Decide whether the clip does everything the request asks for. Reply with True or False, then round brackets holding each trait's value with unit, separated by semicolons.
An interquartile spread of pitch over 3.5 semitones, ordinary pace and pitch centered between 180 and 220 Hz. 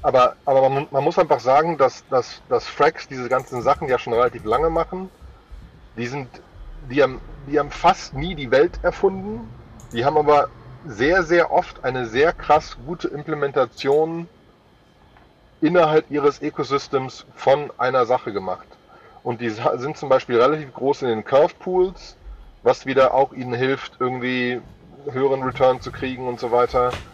False (3.9 semitones; 160 wpm; 135 Hz)